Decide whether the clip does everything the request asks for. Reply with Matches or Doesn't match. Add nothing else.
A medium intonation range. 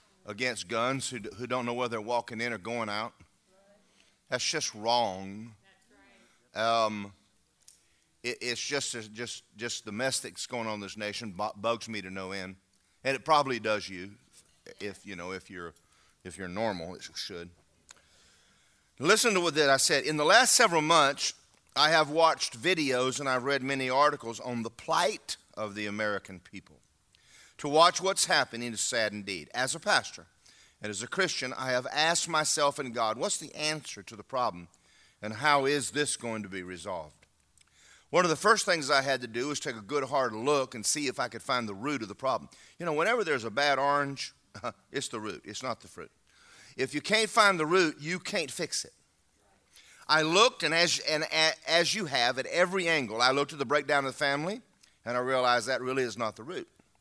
Doesn't match